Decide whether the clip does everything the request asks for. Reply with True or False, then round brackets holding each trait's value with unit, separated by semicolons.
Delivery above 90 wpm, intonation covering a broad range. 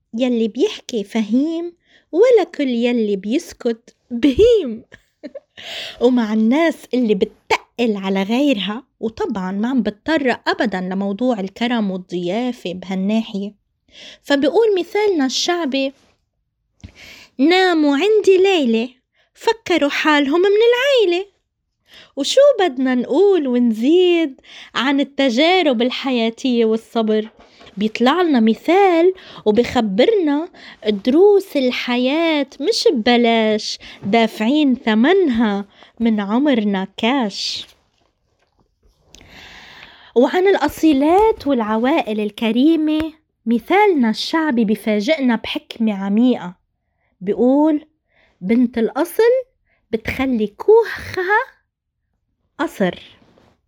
False (75 wpm; 6.2 semitones)